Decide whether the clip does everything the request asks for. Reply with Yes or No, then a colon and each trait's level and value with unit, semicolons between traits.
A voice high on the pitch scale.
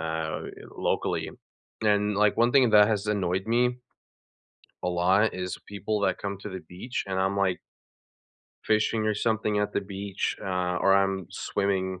No: low, 100 Hz